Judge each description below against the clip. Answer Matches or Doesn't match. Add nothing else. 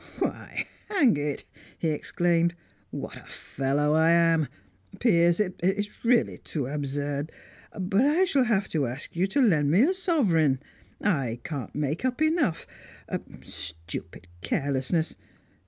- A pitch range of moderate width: Doesn't match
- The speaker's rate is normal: Doesn't match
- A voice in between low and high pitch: Matches